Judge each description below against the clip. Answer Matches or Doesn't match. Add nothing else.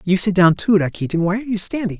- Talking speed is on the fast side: Matches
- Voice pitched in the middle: Doesn't match